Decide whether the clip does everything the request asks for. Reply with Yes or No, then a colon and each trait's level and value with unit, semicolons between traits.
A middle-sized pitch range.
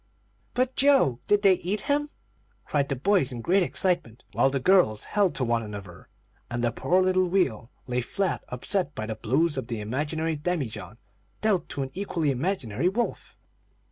No: wide, 7.8 semitones